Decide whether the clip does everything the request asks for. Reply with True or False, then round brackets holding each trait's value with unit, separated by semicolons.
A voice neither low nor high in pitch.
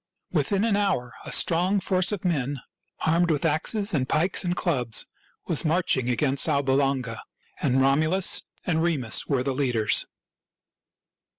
True (155 Hz)